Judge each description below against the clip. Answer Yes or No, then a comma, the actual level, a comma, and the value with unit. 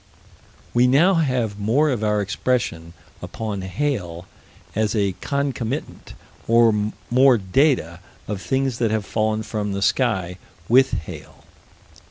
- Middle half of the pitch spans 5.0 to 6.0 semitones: No, average, 4.6 semitones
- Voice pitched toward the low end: Yes, low, 110 Hz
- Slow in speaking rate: Yes, slow, 125 wpm